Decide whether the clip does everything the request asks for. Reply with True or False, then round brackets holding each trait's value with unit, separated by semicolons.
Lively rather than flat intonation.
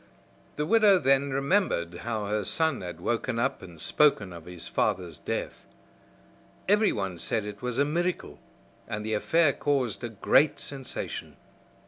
True (6.9 semitones)